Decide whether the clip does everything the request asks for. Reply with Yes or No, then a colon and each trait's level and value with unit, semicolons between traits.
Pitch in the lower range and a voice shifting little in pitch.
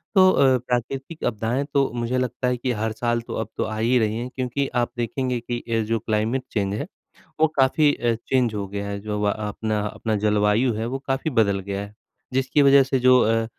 No: low, 120 Hz; average, 3.2 semitones